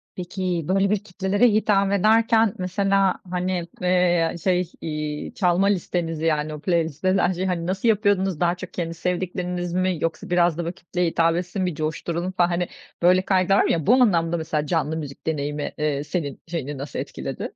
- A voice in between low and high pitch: Yes, medium, 180 Hz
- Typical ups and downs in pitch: No, narrow, 2.3 semitones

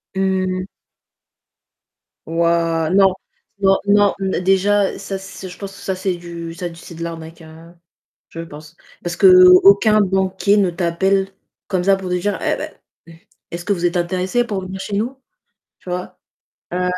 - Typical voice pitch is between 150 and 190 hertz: Yes, medium, 185 Hz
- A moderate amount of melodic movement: No, narrow, 2.3 semitones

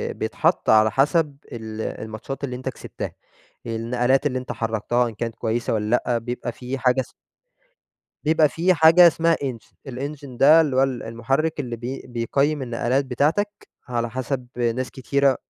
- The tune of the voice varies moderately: Yes, average, 3.2 semitones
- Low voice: Yes, low, 130 Hz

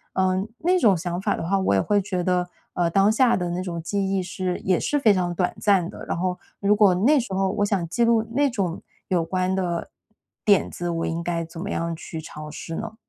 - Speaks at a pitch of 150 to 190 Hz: Yes, medium, 185 Hz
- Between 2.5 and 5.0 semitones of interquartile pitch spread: Yes, average, 2.8 semitones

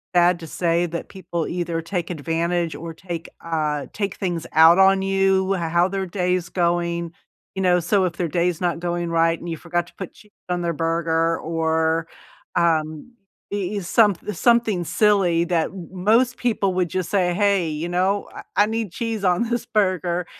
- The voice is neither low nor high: Yes, medium, 175 Hz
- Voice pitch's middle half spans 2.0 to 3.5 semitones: Yes, narrow, 2.5 semitones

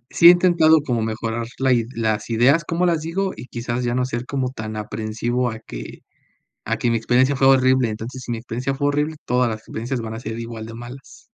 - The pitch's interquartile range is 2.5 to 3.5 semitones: Yes, average, 3.1 semitones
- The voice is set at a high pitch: No, low, 120 Hz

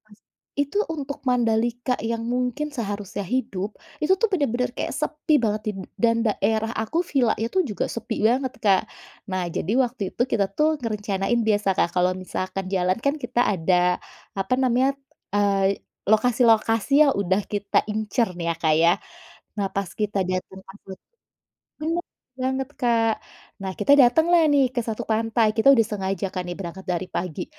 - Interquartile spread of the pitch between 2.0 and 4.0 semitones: No, average, 4.6 semitones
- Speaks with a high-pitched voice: Yes, high, 225 Hz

